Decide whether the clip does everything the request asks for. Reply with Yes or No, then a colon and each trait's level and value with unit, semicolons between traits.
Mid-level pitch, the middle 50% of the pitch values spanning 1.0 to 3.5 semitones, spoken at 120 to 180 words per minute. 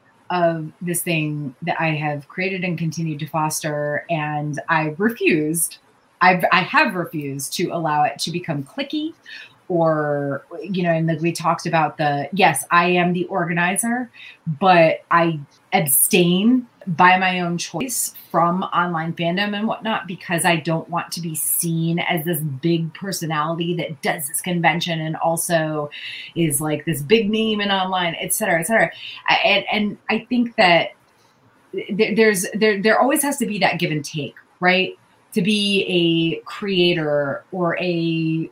Yes: medium, 170 Hz; average, 3.0 semitones; average, 160 wpm